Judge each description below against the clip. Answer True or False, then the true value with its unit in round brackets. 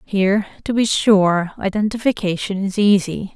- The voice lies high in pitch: True (200 Hz)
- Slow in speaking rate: True (125 wpm)